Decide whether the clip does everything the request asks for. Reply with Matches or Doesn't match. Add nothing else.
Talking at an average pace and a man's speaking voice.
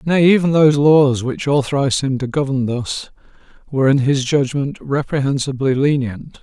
Matches